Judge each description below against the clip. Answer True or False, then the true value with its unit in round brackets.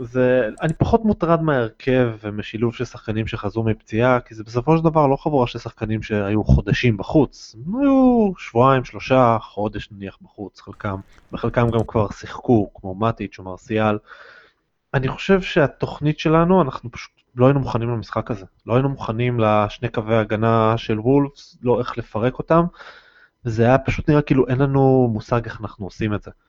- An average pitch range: True (4.1 semitones)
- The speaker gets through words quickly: True (165 wpm)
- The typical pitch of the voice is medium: False (120 Hz)